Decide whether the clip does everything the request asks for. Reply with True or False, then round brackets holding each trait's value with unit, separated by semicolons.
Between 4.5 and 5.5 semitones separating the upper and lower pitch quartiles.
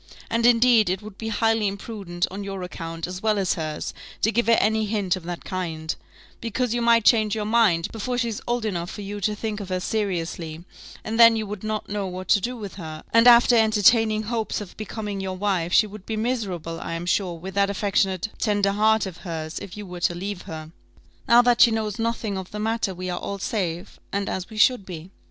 False (3.4 semitones)